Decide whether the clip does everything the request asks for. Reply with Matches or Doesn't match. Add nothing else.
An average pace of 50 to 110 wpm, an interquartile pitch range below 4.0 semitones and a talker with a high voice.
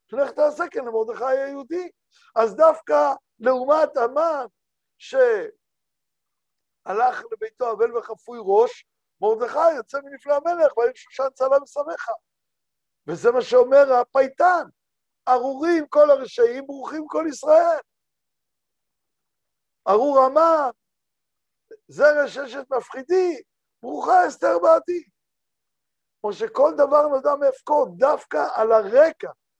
Doesn't match